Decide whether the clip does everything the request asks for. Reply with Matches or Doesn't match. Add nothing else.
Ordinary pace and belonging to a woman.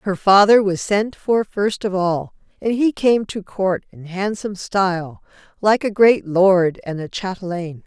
Matches